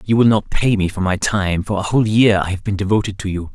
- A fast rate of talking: Yes, fast, 285 wpm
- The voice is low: Yes, low, 100 Hz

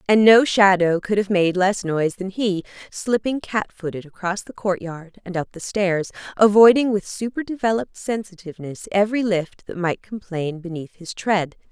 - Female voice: Yes, female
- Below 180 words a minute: Yes, average, 170 wpm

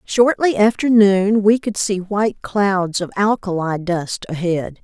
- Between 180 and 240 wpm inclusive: No, average, 150 wpm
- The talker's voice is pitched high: Yes, high, 200 Hz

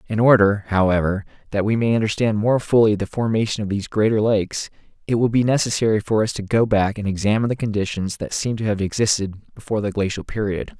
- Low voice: Yes, low, 105 Hz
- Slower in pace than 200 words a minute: No, fast, 205 wpm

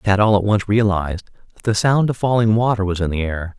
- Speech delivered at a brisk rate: Yes, fast, 250 wpm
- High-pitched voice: No, low, 105 Hz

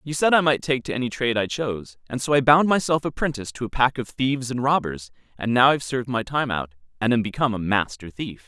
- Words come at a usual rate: No, fast, 255 wpm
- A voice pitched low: Yes, low, 125 Hz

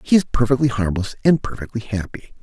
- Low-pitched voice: Yes, low, 115 Hz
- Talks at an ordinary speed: Yes, average, 175 wpm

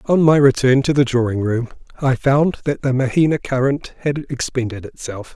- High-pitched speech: No, low, 135 Hz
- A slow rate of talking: No, average, 180 wpm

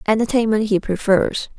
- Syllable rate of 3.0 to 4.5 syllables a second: No, 5.0 syllables/s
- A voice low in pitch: No, high, 210 Hz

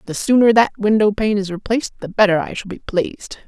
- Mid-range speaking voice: No, high, 205 Hz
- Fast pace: Yes, fast, 225 wpm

